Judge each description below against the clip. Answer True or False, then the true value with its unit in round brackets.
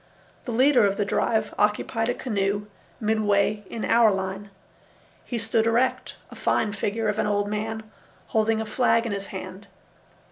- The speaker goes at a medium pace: True (165 wpm)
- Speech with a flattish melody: True (1.9 semitones)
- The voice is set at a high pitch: True (215 Hz)